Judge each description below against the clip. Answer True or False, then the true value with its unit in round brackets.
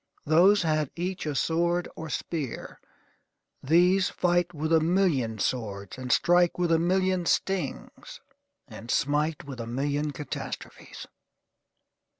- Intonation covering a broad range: False (4.0 semitones)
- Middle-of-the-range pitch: True (160 Hz)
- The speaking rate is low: True (125 wpm)